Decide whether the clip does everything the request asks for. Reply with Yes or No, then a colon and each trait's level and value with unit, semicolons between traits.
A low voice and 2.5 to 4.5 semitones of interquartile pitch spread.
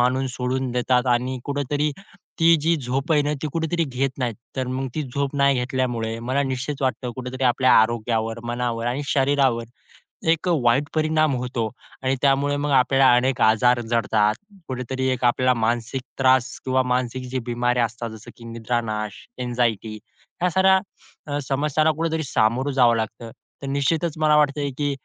Yes: low, 130 Hz; average, 2.9 semitones